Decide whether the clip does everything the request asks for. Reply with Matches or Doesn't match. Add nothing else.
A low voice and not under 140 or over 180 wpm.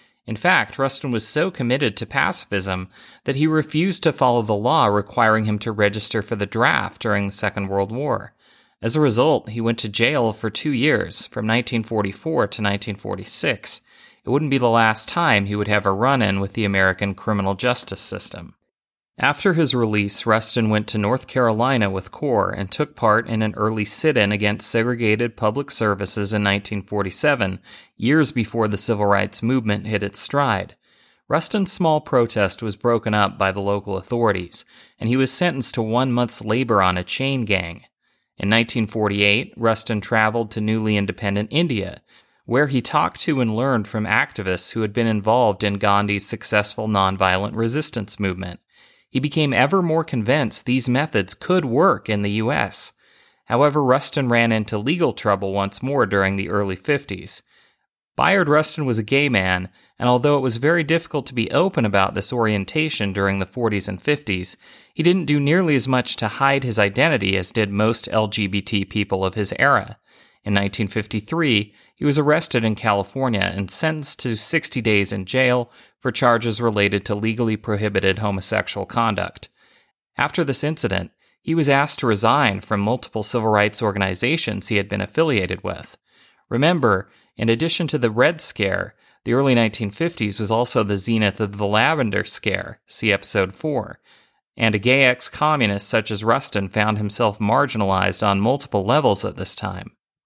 Matches